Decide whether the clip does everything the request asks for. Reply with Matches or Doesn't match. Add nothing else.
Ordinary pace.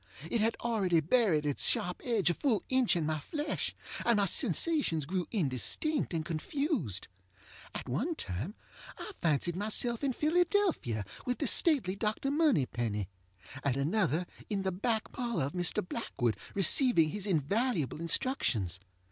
Matches